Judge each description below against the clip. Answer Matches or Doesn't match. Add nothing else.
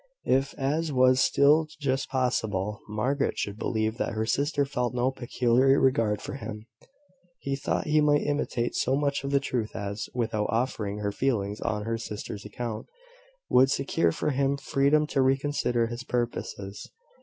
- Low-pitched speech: Matches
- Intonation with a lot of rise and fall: Doesn't match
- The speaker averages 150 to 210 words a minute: Matches